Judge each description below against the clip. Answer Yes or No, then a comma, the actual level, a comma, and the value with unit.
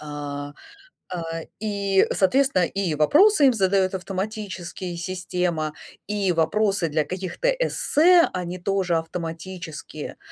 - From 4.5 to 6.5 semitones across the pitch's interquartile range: No, average, 3.6 semitones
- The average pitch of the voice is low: No, medium, 185 Hz